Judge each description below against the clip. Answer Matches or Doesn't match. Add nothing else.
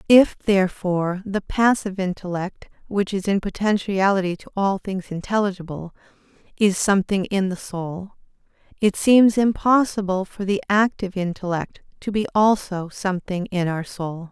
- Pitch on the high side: Matches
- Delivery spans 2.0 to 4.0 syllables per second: Doesn't match